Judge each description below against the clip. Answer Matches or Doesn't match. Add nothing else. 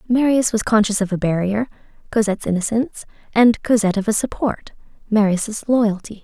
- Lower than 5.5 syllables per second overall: Doesn't match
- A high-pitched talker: Matches